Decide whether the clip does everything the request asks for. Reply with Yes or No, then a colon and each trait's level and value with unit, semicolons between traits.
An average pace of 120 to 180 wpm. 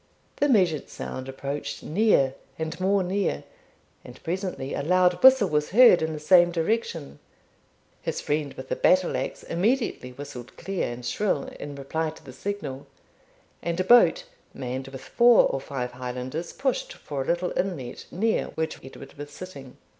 Yes: average, 160 wpm